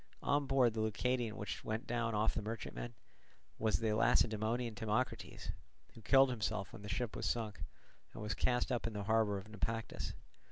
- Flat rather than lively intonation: Yes, narrow, 2.2 semitones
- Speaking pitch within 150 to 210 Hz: No, low, 110 Hz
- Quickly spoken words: No, average, 175 wpm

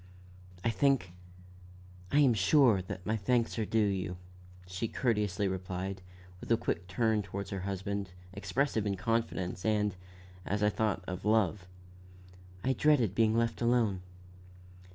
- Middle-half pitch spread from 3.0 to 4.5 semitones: Yes, average, 3.4 semitones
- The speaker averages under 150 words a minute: Yes, average, 140 wpm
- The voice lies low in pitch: Yes, low, 105 Hz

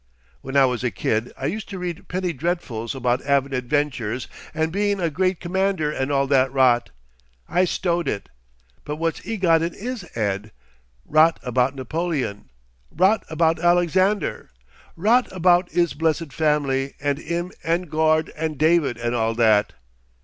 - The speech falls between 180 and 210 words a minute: No, average, 155 wpm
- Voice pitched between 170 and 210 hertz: No, medium, 155 Hz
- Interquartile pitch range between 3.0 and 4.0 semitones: No, average, 4.9 semitones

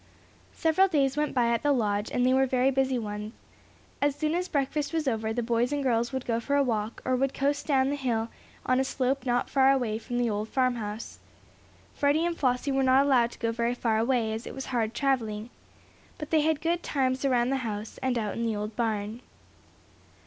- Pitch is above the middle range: Yes, very high, 255 Hz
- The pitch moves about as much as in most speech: Yes, average, 3.2 semitones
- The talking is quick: Yes, fast, 215 wpm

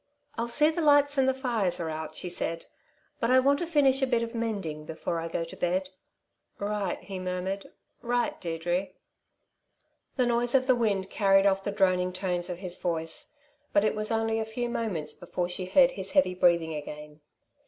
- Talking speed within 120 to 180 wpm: No, average, 195 wpm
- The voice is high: Yes, high, 195 Hz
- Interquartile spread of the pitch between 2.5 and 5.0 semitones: No, wide, 5.4 semitones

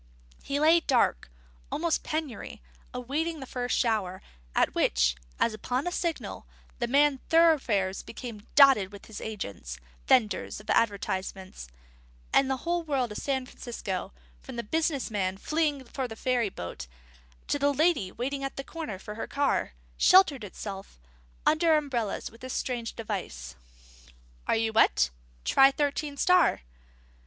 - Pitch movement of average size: No, wide, 5.8 semitones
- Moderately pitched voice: No, very high, 250 Hz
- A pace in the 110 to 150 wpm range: Yes, average, 145 wpm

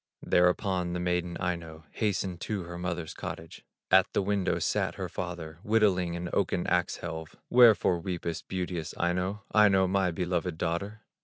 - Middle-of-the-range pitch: No, very low, 90 Hz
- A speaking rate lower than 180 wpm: Yes, average, 155 wpm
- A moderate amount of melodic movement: No, narrow, 1.8 semitones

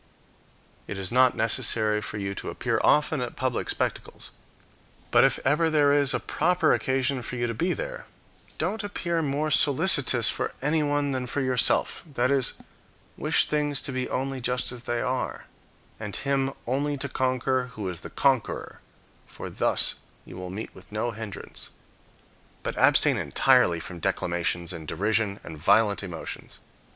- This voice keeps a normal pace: Yes, average, 160 wpm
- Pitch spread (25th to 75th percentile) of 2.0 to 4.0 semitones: No, average, 5.1 semitones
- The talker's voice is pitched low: Yes, low, 130 Hz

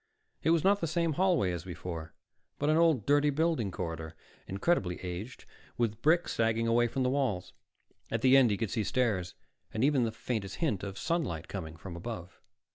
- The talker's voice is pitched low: Yes, low, 115 Hz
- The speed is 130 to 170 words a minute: No, average, 190 wpm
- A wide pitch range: Yes, wide, 8.1 semitones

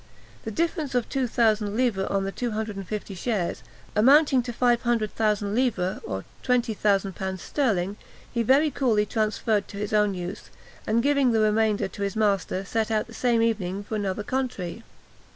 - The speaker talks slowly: No, average, 170 wpm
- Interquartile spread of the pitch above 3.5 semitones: No, average, 3.2 semitones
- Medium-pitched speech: No, high, 215 Hz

